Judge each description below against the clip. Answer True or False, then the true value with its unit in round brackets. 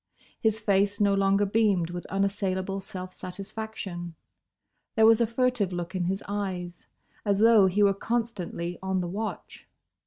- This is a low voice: False (195 Hz)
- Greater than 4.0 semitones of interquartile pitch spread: False (2.7 semitones)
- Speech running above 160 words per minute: False (150 wpm)